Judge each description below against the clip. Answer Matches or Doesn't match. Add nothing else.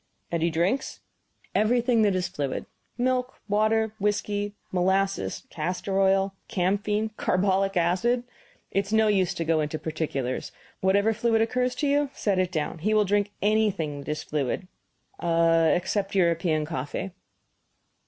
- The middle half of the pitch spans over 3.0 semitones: Matches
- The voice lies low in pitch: Doesn't match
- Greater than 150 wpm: Doesn't match